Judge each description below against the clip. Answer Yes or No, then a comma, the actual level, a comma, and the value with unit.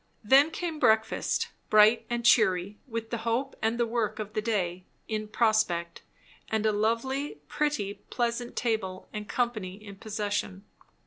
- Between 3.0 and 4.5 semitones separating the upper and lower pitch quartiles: No, narrow, 2.5 semitones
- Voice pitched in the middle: No, high, 220 Hz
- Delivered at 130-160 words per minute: Yes, average, 145 wpm